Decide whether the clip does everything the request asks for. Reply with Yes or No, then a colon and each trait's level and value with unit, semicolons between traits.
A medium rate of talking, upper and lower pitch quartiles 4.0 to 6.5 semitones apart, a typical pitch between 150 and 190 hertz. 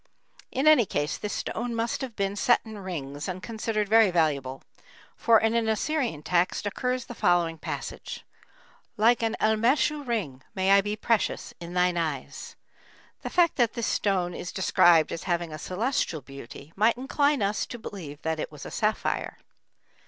No: average, 170 wpm; average, 5.3 semitones; high, 205 Hz